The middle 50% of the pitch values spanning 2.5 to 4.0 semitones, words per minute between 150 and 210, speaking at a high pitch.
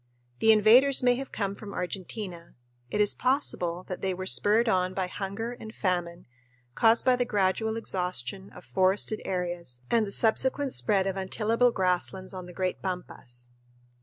Yes: average, 3.5 semitones; average, 165 wpm; high, 195 Hz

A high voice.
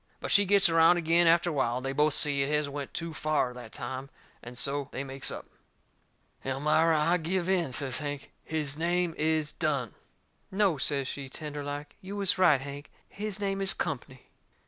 No: medium, 150 Hz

